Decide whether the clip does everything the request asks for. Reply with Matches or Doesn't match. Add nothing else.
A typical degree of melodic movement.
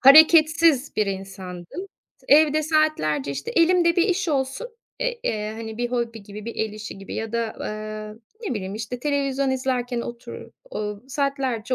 Doesn't match